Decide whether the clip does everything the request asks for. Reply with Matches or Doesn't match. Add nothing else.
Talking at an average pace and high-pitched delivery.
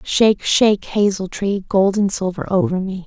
Matches